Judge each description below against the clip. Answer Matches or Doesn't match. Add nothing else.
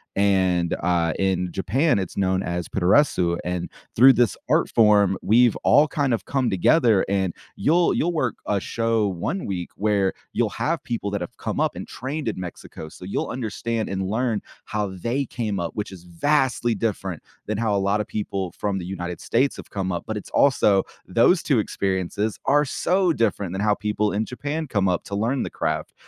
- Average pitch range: Matches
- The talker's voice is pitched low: Matches